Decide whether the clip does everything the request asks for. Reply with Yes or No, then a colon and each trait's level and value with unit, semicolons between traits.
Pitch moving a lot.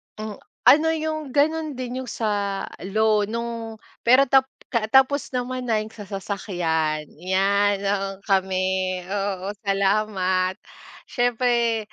No: average, 3.9 semitones